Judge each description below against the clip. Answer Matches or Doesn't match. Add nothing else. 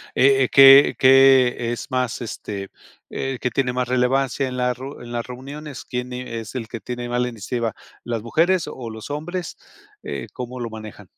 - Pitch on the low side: Matches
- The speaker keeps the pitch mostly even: Matches